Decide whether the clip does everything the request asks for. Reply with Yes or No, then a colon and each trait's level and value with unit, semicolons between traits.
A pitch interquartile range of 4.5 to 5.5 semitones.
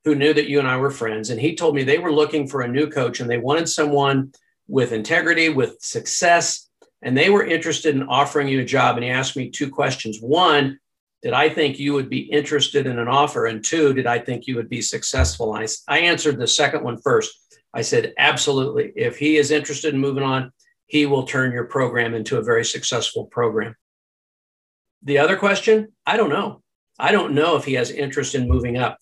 No: average, 3.9 semitones